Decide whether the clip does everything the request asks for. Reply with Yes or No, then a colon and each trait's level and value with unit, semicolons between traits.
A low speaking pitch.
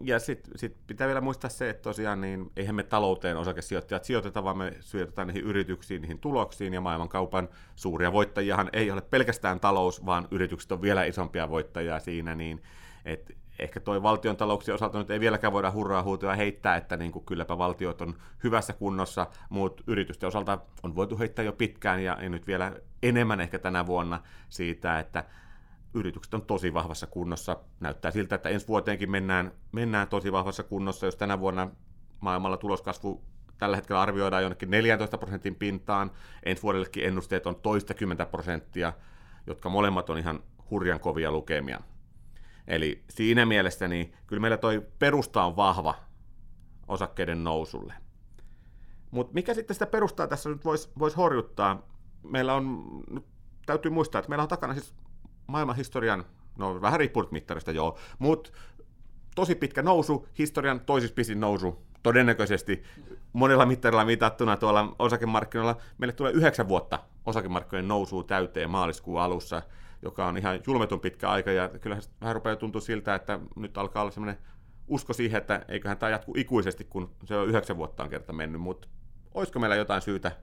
Yes: low, 100 Hz